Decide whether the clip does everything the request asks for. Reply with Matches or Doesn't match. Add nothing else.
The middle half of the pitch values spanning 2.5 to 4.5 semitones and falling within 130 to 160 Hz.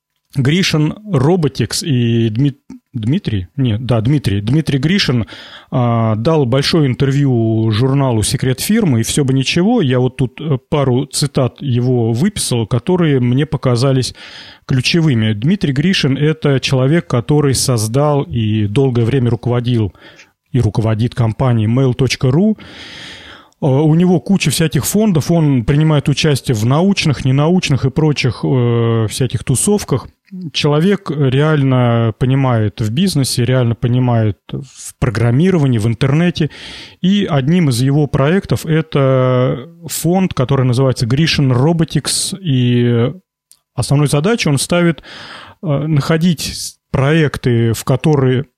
Matches